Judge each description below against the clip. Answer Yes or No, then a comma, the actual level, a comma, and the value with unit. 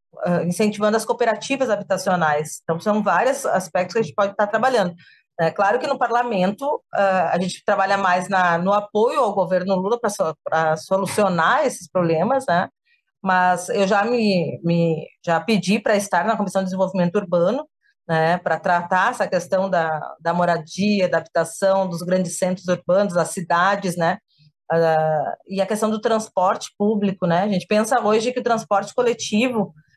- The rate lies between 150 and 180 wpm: Yes, average, 160 wpm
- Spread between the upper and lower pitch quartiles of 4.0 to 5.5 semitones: No, average, 3.6 semitones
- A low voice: No, high, 190 Hz